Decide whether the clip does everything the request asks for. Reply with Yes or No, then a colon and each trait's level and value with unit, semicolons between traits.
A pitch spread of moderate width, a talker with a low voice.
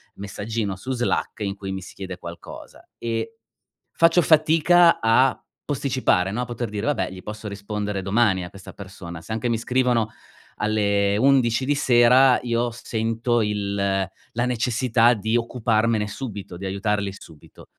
Yes: average, 3.6 semitones; low, 110 Hz